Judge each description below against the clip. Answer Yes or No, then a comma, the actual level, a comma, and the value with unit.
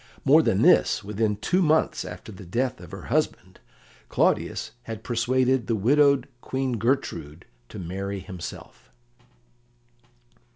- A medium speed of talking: No, slow, 125 wpm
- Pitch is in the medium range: No, low, 115 Hz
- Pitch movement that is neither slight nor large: No, wide, 5.7 semitones